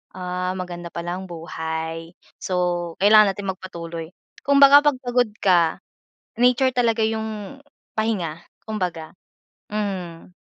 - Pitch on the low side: No, medium, 185 Hz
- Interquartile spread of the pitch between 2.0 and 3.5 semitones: No, average, 4.3 semitones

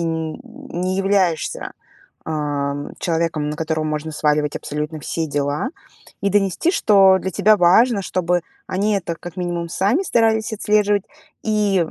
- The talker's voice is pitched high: No, medium, 180 Hz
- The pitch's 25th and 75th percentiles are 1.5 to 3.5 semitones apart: No, average, 4.7 semitones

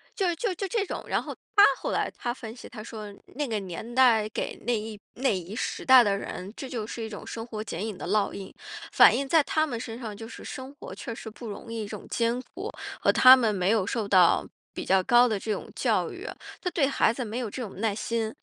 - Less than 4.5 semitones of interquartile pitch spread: Yes, average, 3.4 semitones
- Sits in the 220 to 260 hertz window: Yes, high, 225 Hz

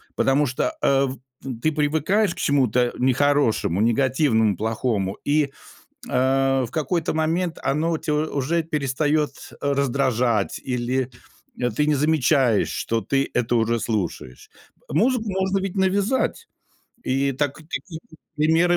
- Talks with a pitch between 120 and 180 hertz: Yes, medium, 140 Hz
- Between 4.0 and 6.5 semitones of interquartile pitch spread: Yes, average, 4.3 semitones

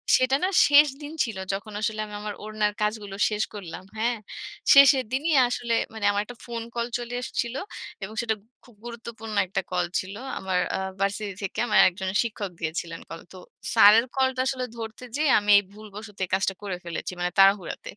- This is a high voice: Yes, high, 215 Hz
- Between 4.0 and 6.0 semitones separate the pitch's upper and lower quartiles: No, average, 3.4 semitones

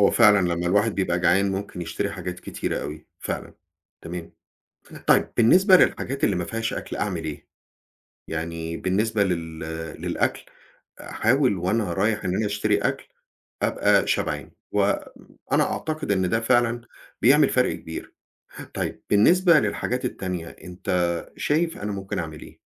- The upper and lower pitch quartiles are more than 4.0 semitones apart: Yes, average, 4.7 semitones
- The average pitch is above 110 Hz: No, low, 100 Hz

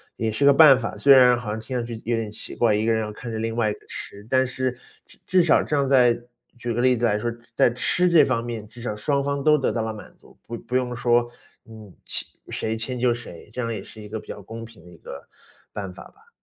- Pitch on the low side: Yes, low, 120 Hz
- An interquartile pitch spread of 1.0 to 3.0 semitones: Yes, narrow, 2.6 semitones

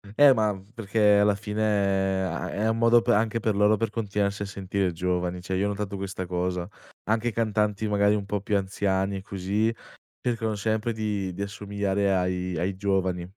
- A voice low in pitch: Yes, low, 100 Hz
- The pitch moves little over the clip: Yes, narrow, 2.0 semitones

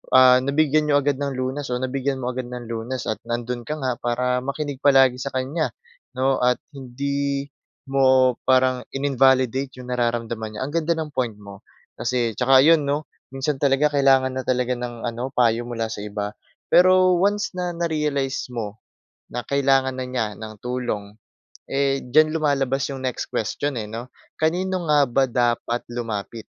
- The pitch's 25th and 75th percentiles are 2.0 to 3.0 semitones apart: Yes, narrow, 2.6 semitones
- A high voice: No, low, 130 Hz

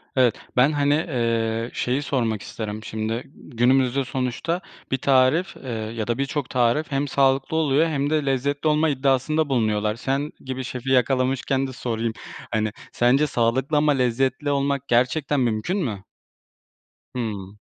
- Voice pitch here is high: No, low, 130 Hz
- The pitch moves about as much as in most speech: Yes, average, 3.3 semitones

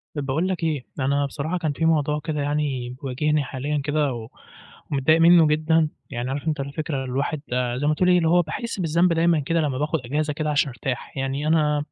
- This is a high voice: No, medium, 150 Hz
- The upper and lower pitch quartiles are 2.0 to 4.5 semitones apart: Yes, narrow, 2.6 semitones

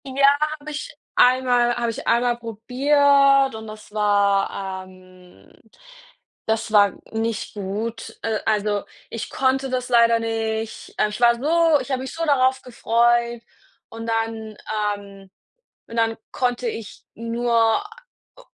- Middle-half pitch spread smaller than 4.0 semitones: Yes, average, 2.9 semitones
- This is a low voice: No, high, 230 Hz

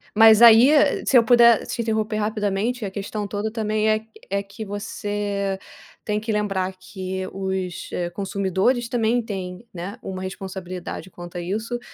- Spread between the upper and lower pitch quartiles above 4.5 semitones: No, narrow, 2.6 semitones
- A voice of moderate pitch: No, high, 205 Hz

